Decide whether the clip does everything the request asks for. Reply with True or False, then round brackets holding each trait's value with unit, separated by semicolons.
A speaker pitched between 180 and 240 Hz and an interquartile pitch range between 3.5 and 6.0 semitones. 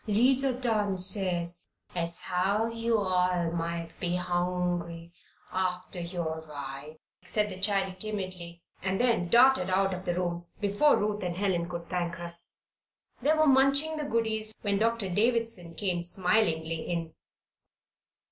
True (185 Hz; 4.0 semitones)